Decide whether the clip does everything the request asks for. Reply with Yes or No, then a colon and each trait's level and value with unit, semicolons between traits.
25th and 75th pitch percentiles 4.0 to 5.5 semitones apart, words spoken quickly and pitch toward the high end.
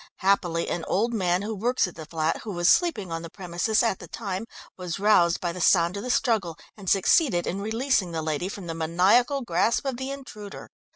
Yes: average, 4.7 semitones; fast, 215 wpm; high, 195 Hz